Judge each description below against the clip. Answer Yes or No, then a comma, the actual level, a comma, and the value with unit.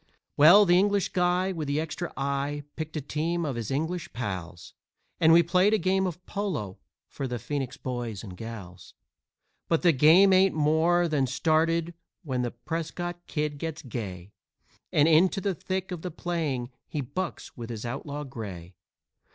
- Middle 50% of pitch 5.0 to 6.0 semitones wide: Yes, wide, 5.6 semitones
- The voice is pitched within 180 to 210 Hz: No, medium, 155 Hz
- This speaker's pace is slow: No, average, 170 wpm